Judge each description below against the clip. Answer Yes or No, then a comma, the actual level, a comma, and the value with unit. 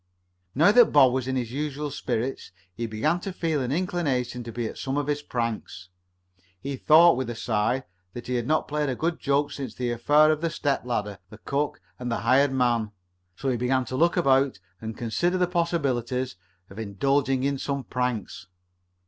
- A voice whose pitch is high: No, low, 130 Hz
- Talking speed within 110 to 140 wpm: No, average, 195 wpm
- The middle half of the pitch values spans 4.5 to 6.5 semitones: No, average, 3.7 semitones